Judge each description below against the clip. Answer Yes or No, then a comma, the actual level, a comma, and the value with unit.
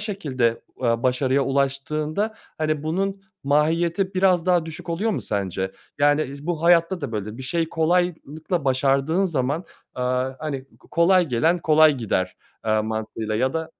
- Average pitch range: Yes, average, 4.7 semitones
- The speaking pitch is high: No, medium, 150 Hz